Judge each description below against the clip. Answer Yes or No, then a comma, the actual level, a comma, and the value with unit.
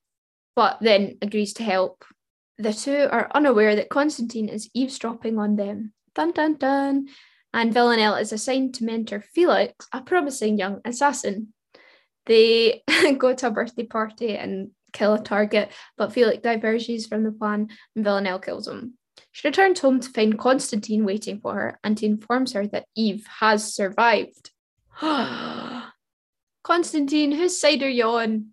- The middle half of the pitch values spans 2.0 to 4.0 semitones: No, average, 4.4 semitones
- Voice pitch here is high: Yes, high, 230 Hz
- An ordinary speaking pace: Yes, average, 150 wpm